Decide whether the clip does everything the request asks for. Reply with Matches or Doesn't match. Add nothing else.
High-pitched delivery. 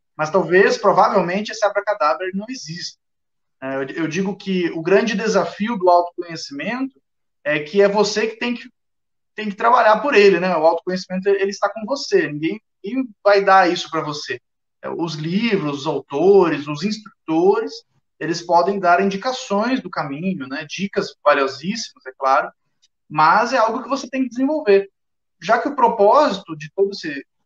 Matches